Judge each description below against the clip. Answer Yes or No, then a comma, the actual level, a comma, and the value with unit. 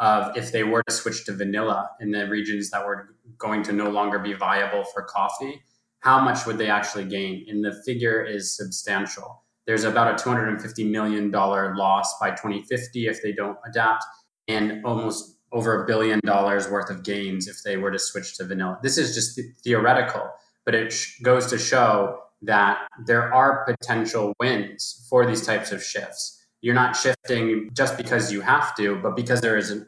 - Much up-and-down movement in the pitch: No, narrow, 2.6 semitones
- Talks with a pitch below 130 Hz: Yes, low, 110 Hz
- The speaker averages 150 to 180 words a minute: No, average, 190 wpm